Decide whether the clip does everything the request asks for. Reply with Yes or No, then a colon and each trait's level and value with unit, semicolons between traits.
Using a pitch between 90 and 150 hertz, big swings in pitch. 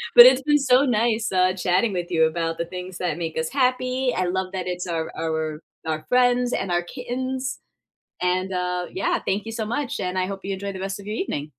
No: high, 190 Hz; wide, 5.7 semitones